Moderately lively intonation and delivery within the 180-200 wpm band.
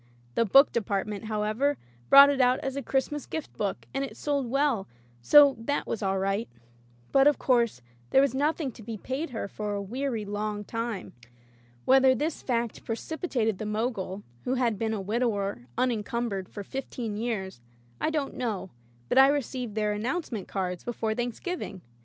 Yes: average, 4.5 semitones; average, 185 wpm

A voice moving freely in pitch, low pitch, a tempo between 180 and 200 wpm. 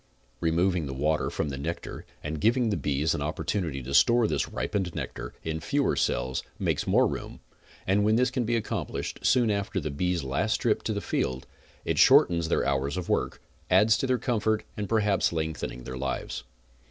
Yes: wide, 7.0 semitones; very low, 90 Hz; average, 190 wpm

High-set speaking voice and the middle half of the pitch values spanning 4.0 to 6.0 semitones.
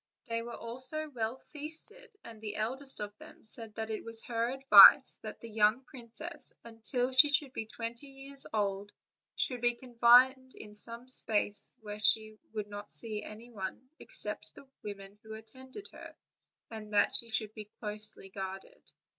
No: high, 230 Hz; average, 3.4 semitones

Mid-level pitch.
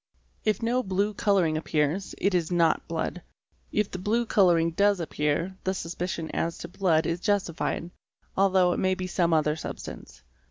Yes: medium, 180 Hz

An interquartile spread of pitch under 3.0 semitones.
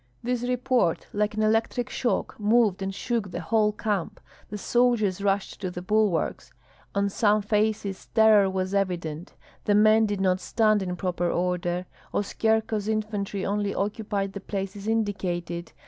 Yes: narrow, 2.4 semitones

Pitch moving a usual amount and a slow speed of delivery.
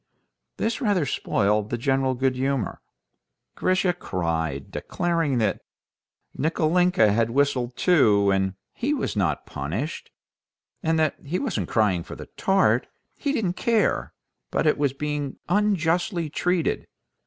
No: wide, 8.5 semitones; slow, 120 wpm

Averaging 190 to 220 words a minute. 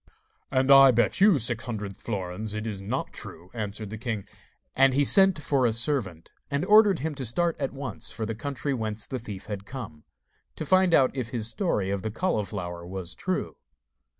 Yes: average, 195 wpm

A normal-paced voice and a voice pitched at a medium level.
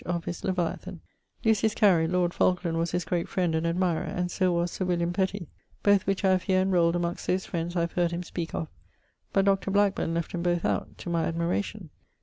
No: fast, 215 wpm; medium, 175 Hz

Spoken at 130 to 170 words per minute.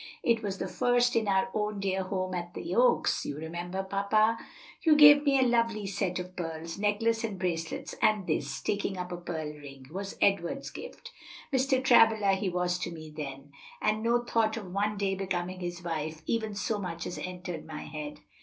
No: average, 190 wpm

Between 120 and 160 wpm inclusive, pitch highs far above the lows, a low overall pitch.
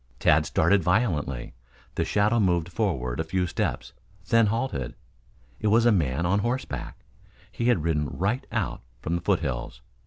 Yes: average, 155 wpm; wide, 6.4 semitones; very low, 90 Hz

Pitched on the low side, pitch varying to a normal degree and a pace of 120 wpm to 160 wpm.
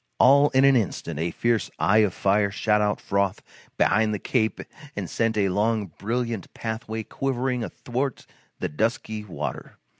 Yes: low, 110 Hz; average, 3.0 semitones; average, 155 wpm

